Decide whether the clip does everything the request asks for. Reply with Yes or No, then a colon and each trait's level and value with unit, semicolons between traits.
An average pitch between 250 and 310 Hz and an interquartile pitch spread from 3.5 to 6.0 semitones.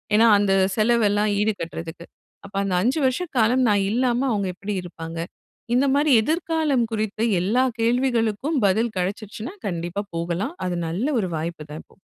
No: high, 215 Hz; average, 5.2 semitones